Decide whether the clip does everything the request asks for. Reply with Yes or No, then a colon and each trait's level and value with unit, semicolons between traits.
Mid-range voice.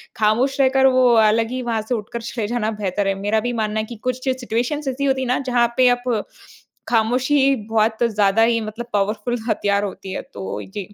No: high, 230 Hz